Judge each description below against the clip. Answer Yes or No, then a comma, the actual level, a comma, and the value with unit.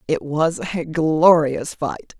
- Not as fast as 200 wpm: Yes, slow, 135 wpm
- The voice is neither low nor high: Yes, medium, 150 Hz